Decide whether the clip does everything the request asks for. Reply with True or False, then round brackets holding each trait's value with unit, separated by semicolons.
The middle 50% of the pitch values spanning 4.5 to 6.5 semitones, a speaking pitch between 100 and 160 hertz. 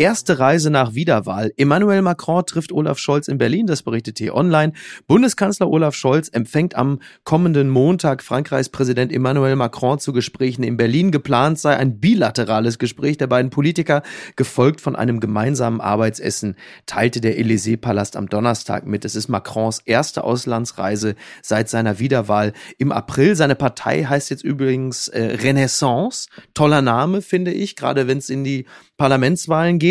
True (4.8 semitones; 135 Hz)